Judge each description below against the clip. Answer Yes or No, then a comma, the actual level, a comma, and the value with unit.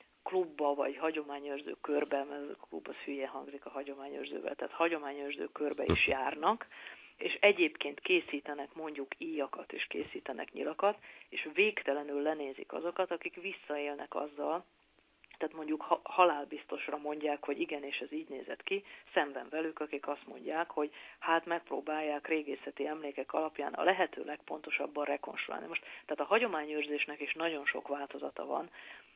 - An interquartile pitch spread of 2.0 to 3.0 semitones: Yes, narrow, 2.5 semitones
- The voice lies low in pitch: No, medium, 150 Hz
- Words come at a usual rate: Yes, average, 140 wpm